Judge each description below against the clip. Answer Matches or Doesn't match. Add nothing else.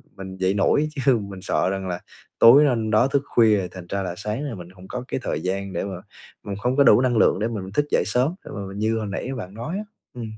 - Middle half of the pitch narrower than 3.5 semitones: Doesn't match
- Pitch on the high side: Doesn't match